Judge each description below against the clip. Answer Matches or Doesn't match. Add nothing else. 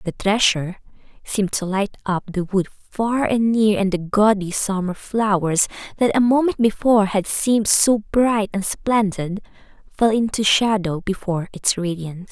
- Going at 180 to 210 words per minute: Doesn't match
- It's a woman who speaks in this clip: Matches